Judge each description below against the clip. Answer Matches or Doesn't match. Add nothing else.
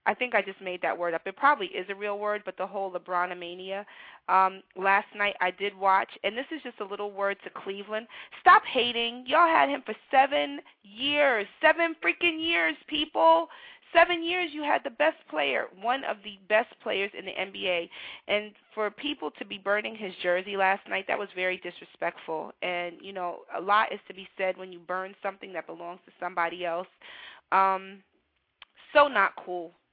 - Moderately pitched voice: Doesn't match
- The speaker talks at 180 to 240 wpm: Matches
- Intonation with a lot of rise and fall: Matches